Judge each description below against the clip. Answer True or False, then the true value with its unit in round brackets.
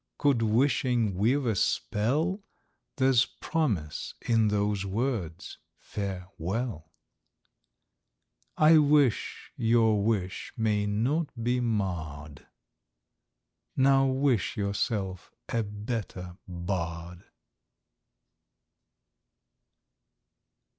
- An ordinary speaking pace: False (75 wpm)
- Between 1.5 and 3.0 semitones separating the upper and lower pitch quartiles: False (5.3 semitones)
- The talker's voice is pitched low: True (110 Hz)